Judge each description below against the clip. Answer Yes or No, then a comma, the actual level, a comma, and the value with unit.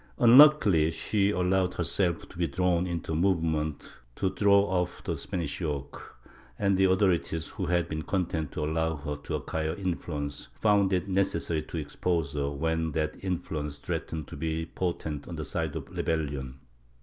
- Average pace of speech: Yes, average, 165 wpm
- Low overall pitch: Yes, very low, 80 Hz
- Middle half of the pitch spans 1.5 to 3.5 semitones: Yes, average, 3.1 semitones